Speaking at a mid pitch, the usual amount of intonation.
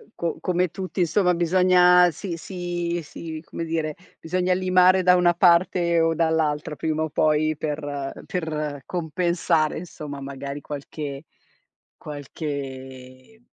Yes: medium, 165 Hz; average, 3.2 semitones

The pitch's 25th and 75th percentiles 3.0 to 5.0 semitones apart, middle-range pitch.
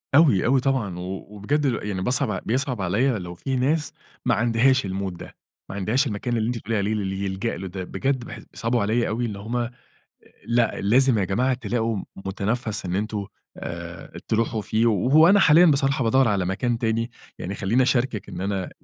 No: average, 4.5 semitones; low, 115 Hz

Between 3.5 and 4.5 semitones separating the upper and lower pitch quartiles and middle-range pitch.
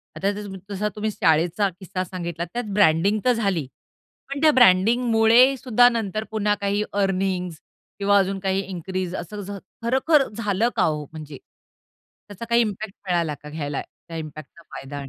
No: average, 4.2 semitones; high, 195 Hz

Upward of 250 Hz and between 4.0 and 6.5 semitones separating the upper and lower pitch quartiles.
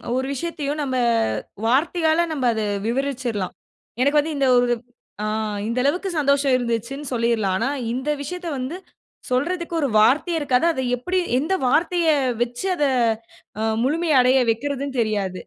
Yes: very high, 275 Hz; average, 4.4 semitones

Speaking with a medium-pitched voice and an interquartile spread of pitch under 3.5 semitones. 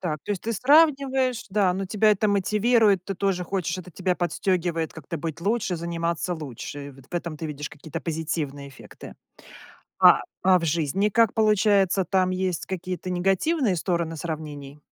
No: medium, 180 Hz; average, 3.8 semitones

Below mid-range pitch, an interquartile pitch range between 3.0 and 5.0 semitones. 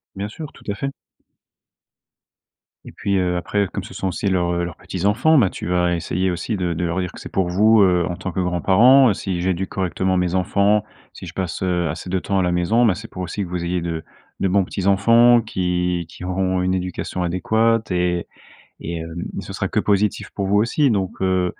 No: very low, 95 Hz; narrow, 2.4 semitones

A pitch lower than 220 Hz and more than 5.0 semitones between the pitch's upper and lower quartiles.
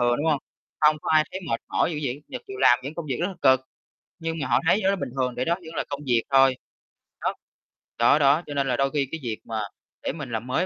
No: medium, 140 Hz; average, 4.2 semitones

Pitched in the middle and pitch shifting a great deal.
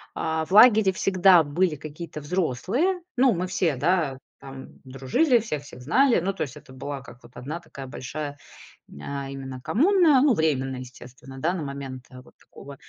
Yes: medium, 150 Hz; wide, 6.0 semitones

